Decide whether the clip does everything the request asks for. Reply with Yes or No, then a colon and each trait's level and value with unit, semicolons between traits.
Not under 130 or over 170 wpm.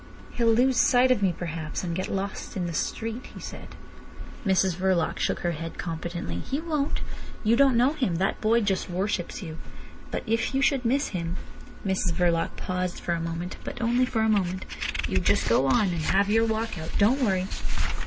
No: average, 195 wpm